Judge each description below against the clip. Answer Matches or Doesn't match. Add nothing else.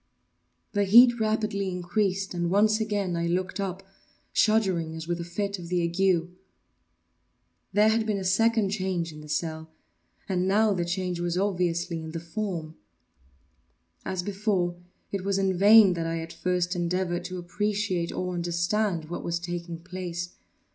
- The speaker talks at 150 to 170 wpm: Matches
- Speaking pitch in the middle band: Matches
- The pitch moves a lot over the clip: Doesn't match